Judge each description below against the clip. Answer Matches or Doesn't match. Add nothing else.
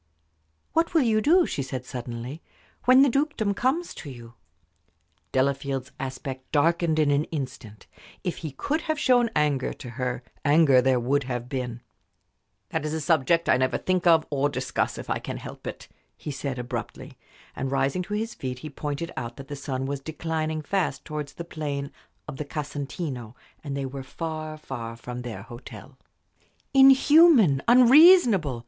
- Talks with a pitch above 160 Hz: Doesn't match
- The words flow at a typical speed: Matches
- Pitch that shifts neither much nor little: Matches